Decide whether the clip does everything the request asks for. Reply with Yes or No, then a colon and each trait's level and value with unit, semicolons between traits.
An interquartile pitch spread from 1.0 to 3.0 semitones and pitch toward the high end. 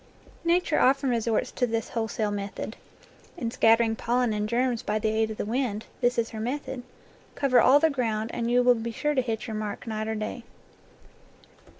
Yes: narrow, 2.4 semitones; high, 230 Hz